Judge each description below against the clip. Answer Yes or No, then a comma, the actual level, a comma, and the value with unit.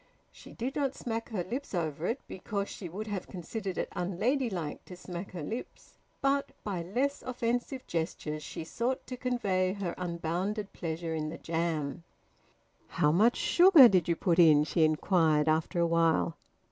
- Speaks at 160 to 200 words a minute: Yes, average, 165 wpm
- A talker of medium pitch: Yes, medium, 180 Hz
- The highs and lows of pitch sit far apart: Yes, wide, 5.9 semitones